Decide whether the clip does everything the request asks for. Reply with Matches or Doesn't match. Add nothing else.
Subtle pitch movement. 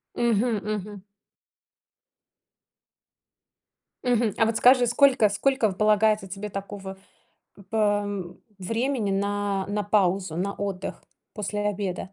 Matches